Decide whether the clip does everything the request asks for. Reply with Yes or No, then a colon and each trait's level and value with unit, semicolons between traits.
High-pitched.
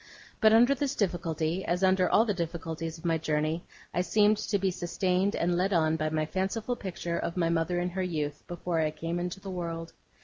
No: medium, 175 Hz